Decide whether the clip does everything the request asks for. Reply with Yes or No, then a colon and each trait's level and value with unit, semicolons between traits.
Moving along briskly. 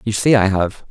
Yes: fast, 265 wpm